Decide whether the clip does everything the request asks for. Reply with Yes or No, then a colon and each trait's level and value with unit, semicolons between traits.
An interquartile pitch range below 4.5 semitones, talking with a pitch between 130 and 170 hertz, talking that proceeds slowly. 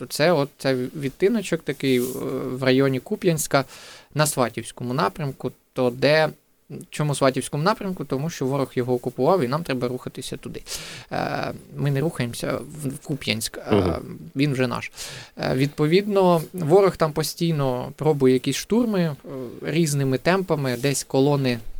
No: average, 3.7 semitones; medium, 140 Hz; average, 125 wpm